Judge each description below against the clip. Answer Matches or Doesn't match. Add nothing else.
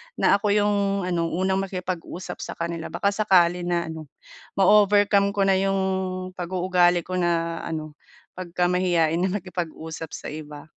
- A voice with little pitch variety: Matches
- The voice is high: Doesn't match